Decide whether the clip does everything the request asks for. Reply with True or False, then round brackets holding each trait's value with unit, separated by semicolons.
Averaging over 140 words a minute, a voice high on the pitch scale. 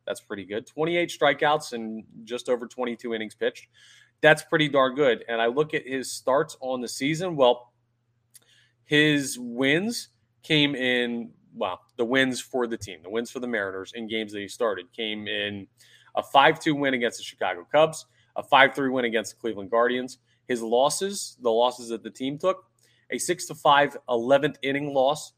False (180 wpm; 125 Hz)